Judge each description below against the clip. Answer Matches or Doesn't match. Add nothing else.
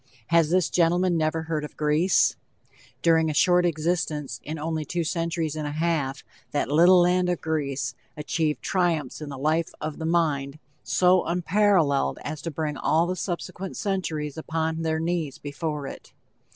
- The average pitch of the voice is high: Doesn't match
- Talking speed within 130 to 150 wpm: Doesn't match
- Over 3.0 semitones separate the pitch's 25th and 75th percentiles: Doesn't match